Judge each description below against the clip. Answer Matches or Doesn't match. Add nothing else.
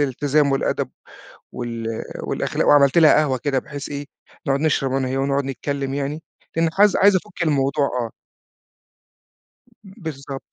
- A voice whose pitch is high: Doesn't match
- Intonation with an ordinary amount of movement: Doesn't match